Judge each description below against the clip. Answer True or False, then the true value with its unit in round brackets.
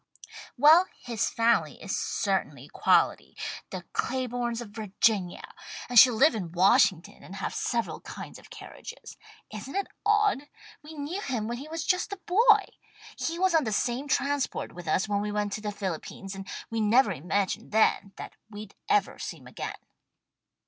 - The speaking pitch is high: True (230 Hz)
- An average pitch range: False (6.5 semitones)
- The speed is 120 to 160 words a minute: False (170 wpm)